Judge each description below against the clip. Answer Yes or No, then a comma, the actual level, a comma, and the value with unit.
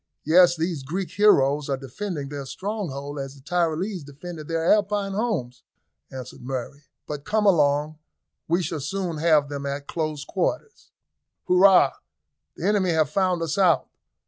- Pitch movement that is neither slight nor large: Yes, average, 4.8 semitones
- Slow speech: No, average, 145 wpm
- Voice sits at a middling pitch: Yes, medium, 160 Hz